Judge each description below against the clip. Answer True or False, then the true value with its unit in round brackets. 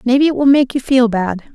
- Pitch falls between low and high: False (250 Hz)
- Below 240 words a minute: False (275 wpm)